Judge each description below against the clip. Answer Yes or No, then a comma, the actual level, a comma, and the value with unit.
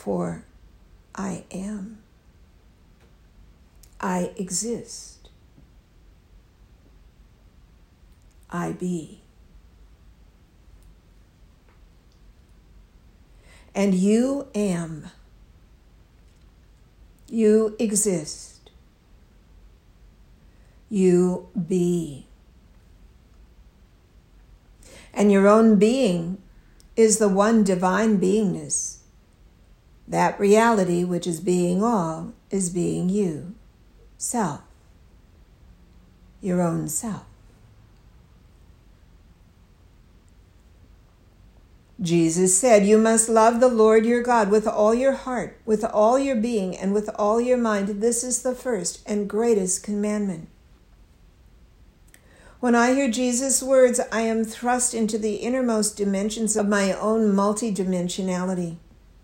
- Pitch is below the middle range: No, medium, 180 Hz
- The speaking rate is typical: No, slow, 80 wpm